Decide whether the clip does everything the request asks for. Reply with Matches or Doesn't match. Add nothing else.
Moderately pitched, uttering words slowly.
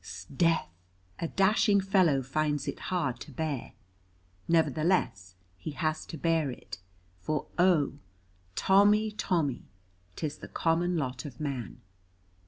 Matches